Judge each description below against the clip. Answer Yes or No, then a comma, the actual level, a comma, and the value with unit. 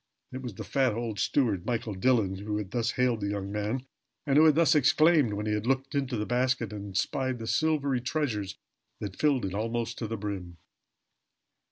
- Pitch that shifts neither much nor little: Yes, average, 4.1 semitones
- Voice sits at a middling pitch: No, low, 115 Hz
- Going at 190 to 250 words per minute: Yes, average, 200 wpm